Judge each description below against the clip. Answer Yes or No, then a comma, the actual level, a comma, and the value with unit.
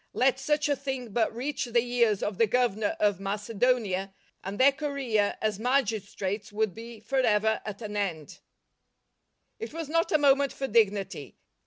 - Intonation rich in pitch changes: No, average, 4.5 semitones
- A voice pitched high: Yes, high, 230 Hz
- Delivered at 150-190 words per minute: Yes, average, 165 wpm